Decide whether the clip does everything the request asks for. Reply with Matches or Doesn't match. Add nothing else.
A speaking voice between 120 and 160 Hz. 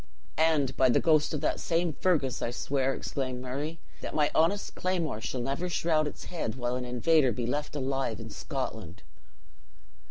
Matches